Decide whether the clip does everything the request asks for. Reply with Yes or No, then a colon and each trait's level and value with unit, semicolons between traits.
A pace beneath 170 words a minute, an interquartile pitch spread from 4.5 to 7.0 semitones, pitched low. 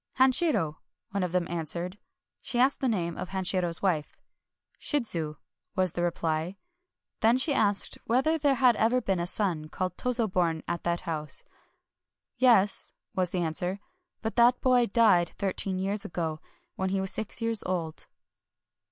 No: average, 160 wpm; average, 5.2 semitones; high, 190 Hz